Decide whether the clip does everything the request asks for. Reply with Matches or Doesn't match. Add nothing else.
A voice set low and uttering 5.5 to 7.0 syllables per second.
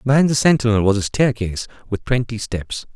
Matches